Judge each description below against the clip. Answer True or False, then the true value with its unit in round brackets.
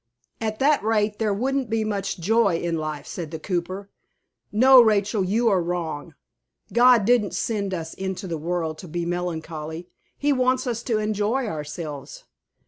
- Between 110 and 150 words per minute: False (160 wpm)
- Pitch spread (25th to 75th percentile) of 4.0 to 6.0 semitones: True (4.9 semitones)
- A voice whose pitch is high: True (200 Hz)